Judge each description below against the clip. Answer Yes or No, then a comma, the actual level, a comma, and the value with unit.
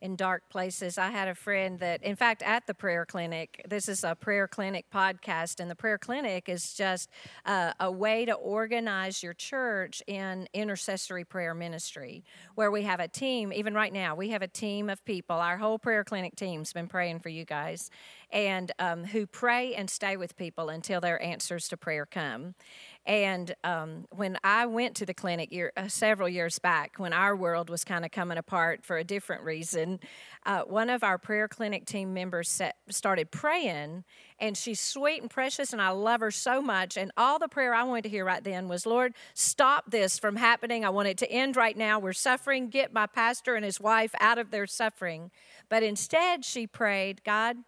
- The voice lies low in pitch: No, high, 195 Hz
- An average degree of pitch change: Yes, average, 3.7 semitones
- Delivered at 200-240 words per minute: Yes, fast, 205 wpm